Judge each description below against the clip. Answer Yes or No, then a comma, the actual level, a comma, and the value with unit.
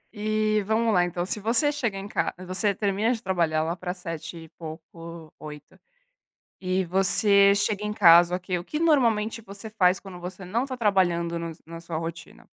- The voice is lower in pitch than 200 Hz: Yes, high, 190 Hz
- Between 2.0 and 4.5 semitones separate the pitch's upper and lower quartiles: Yes, average, 3.9 semitones